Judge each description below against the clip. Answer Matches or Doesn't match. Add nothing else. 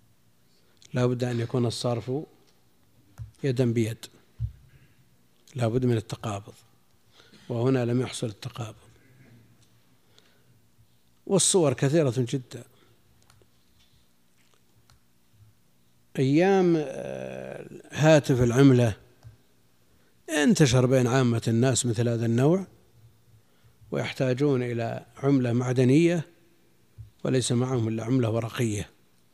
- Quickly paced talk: Doesn't match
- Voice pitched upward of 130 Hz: Doesn't match